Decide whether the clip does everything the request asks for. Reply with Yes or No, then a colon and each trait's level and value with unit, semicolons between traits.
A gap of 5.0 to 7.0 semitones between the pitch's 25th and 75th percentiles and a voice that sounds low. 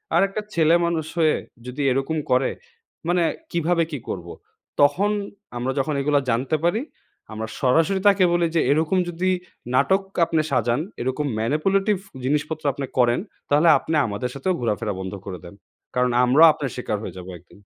No: average, 5.3 semitones; medium, 150 Hz